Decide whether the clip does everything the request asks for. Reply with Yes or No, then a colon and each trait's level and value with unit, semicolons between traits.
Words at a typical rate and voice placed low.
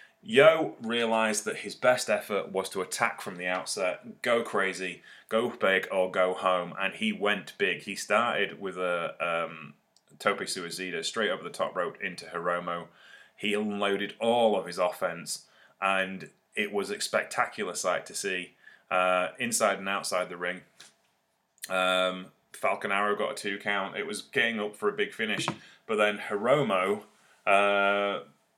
Yes: average, 160 wpm; low, 100 Hz